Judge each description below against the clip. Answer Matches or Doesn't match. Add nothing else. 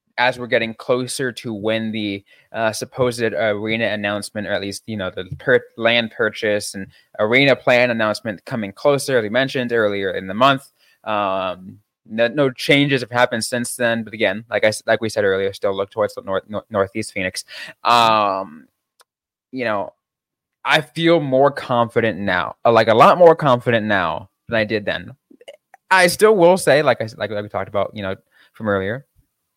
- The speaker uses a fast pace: Doesn't match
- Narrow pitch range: Doesn't match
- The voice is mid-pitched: Doesn't match